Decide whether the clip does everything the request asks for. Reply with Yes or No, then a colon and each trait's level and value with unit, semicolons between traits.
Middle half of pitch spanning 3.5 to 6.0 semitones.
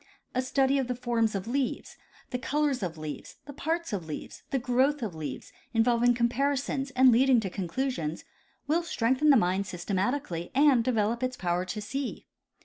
Yes: wide, 5.4 semitones